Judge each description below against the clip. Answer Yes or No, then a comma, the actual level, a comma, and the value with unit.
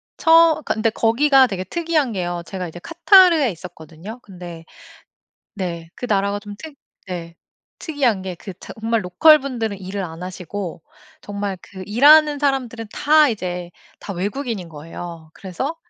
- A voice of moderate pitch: No, high, 205 Hz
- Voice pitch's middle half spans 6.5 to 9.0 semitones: Yes, wide, 7.4 semitones